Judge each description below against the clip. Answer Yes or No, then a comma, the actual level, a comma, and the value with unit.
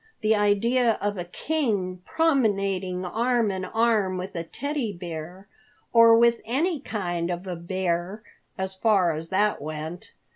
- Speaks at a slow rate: No, average, 145 wpm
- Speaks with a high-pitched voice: Yes, high, 195 Hz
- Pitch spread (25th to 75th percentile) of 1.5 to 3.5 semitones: No, average, 4.3 semitones